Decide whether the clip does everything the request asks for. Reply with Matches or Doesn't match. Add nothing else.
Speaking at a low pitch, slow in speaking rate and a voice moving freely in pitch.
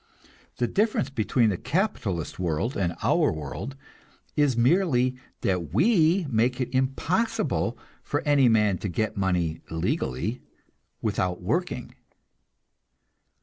Matches